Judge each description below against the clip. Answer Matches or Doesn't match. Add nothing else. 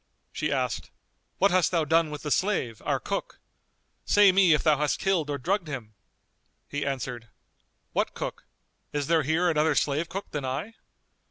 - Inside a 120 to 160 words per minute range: Doesn't match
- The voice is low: Doesn't match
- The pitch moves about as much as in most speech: Matches